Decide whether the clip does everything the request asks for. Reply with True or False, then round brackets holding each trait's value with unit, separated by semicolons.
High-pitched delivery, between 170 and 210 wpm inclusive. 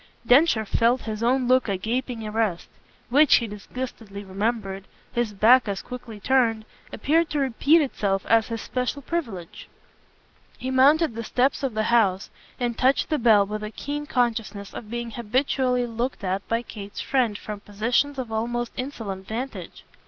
False (235 Hz; 160 wpm)